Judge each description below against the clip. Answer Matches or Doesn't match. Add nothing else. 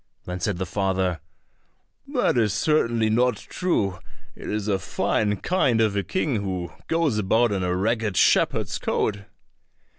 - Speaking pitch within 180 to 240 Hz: Doesn't match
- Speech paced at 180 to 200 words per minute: Doesn't match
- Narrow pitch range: Doesn't match